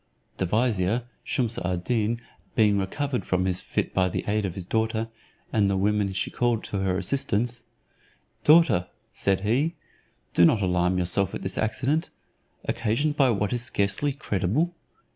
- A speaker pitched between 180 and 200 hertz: No, low, 105 Hz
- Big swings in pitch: No, average, 4.3 semitones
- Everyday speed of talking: Yes, average, 160 wpm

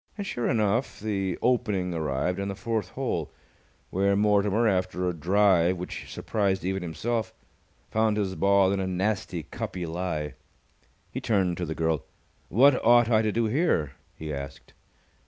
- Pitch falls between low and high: No, very low, 95 Hz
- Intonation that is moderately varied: Yes, average, 3.5 semitones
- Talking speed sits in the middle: Yes, average, 155 wpm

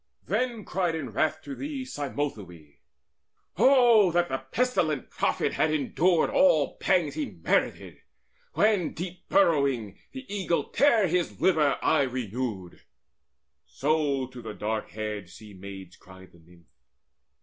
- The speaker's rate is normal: No, slow, 130 wpm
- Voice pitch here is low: No, medium, 150 Hz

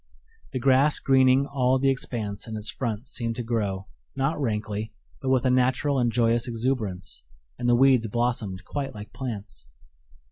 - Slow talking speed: No, average, 165 wpm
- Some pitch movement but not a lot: Yes, average, 3.5 semitones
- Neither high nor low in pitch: No, low, 120 Hz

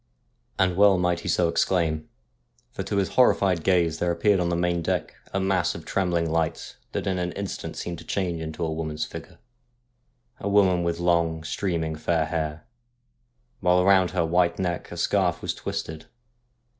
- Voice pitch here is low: Yes, very low, 85 Hz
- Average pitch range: No, narrow, 2.1 semitones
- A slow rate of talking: No, average, 180 wpm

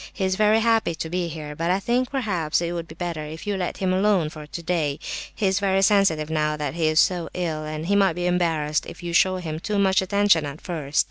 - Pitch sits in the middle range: Yes, medium, 175 Hz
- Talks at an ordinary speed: No, fast, 240 wpm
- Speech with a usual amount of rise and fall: Yes, average, 3.6 semitones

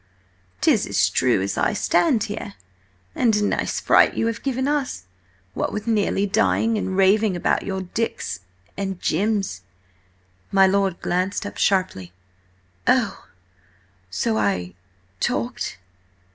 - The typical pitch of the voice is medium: No, high, 195 Hz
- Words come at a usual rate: No, slow, 130 wpm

